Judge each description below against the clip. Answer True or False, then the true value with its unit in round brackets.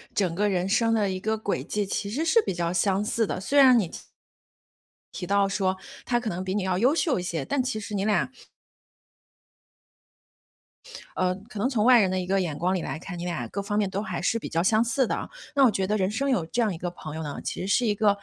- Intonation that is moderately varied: True (3.5 semitones)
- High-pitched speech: True (200 Hz)